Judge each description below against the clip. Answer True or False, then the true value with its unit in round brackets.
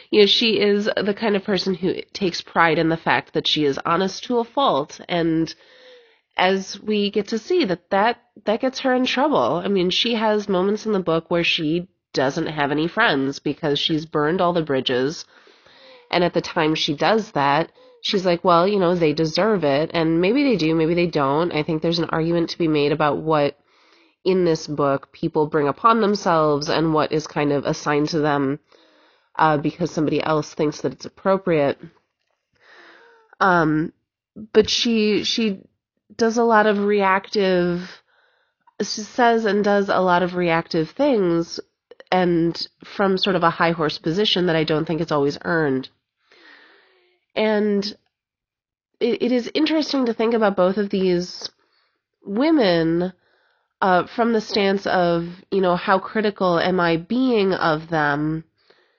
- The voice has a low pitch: False (180 Hz)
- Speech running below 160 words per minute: False (170 wpm)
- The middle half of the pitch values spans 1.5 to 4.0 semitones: False (5.1 semitones)